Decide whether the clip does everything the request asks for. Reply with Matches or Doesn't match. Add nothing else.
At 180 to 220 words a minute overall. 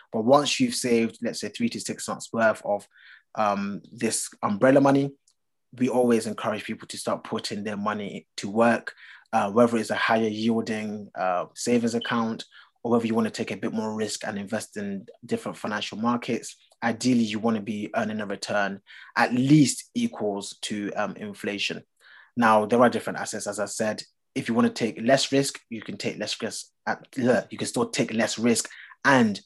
Matches